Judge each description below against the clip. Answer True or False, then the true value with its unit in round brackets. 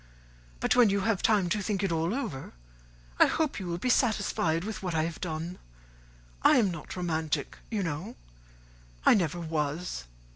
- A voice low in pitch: False (180 Hz)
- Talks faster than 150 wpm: True (180 wpm)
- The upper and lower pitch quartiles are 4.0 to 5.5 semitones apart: True (4.5 semitones)